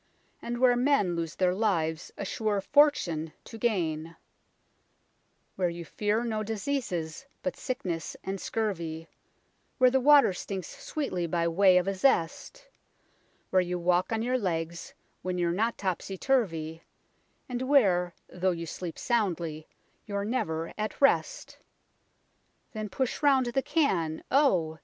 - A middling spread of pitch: No, wide, 6.1 semitones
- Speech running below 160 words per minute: Yes, average, 140 wpm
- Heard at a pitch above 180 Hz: Yes, high, 190 Hz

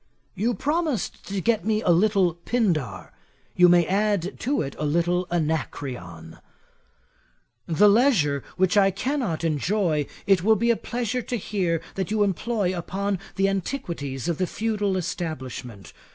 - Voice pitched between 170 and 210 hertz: Yes, high, 190 Hz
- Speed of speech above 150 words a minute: No, average, 145 wpm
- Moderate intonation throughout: Yes, average, 4.8 semitones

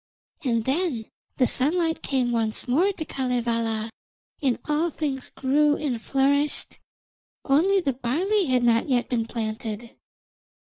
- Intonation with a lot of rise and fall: No, average, 4.3 semitones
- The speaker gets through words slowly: Yes, slow, 130 wpm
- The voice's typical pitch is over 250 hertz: Yes, very high, 260 Hz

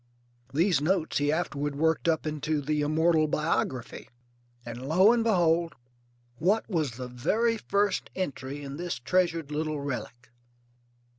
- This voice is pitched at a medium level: Yes, medium, 155 Hz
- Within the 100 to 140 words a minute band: Yes, slow, 135 wpm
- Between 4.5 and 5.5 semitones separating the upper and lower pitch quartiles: No, average, 3.6 semitones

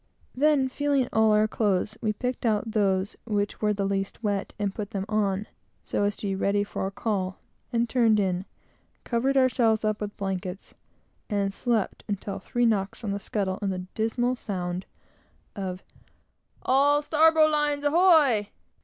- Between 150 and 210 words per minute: Yes, average, 160 wpm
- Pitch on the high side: Yes, high, 215 Hz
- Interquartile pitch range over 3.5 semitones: Yes, average, 3.9 semitones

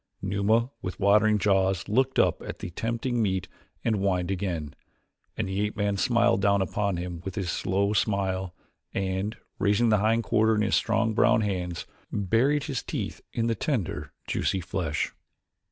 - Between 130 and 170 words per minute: Yes, average, 160 wpm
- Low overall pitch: Yes, low, 100 Hz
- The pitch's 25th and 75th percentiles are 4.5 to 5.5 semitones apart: No, average, 2.7 semitones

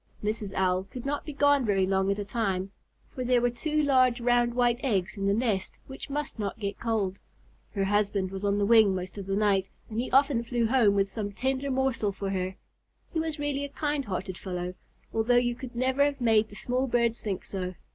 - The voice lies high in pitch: Yes, high, 225 Hz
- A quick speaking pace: Yes, fast, 220 wpm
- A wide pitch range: No, average, 4.6 semitones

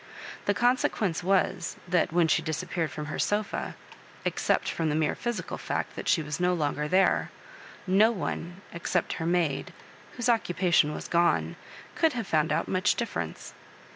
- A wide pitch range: No, average, 4.0 semitones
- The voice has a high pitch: No, medium, 175 Hz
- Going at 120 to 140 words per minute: No, average, 165 wpm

